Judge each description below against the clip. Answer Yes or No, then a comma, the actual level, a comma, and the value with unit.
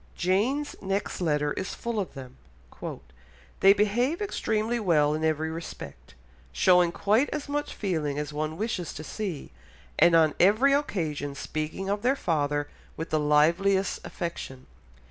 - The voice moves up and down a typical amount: No, wide, 5.7 semitones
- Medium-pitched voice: Yes, medium, 175 Hz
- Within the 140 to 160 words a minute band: Yes, average, 145 wpm